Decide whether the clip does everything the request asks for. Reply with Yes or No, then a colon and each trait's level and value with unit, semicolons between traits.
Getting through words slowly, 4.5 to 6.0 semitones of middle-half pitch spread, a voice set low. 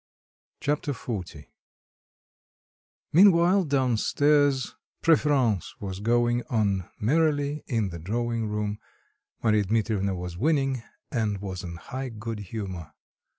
Yes: slow, 110 wpm; wide, 5.6 semitones; low, 115 Hz